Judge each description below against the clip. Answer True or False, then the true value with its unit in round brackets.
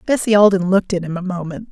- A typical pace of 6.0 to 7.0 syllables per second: True (6.9 syllables/s)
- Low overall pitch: False (190 Hz)